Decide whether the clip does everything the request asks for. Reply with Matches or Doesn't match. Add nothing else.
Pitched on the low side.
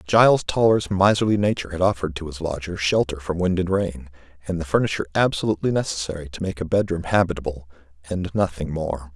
Matches